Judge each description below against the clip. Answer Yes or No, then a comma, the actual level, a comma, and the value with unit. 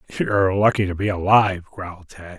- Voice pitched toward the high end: No, very low, 95 Hz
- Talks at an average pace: Yes, average, 175 wpm